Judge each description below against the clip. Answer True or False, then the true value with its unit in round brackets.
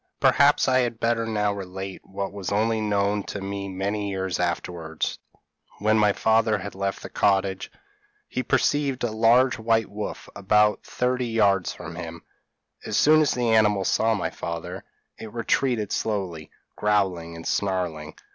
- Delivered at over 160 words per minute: False (155 wpm)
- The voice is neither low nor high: False (105 Hz)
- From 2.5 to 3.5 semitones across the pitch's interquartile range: True (2.9 semitones)